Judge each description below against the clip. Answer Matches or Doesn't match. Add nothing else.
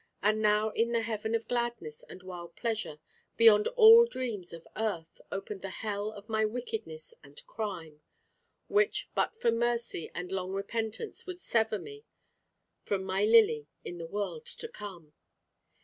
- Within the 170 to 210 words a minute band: Doesn't match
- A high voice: Matches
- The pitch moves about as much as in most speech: Matches